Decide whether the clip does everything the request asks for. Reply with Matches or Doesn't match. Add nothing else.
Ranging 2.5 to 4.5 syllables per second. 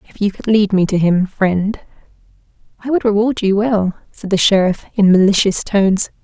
Doesn't match